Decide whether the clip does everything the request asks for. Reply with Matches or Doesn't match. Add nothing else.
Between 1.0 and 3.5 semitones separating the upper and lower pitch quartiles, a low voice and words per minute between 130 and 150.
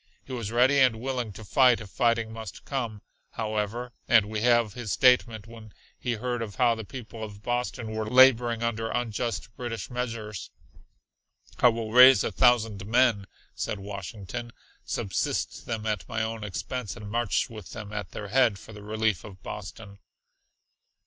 Doesn't match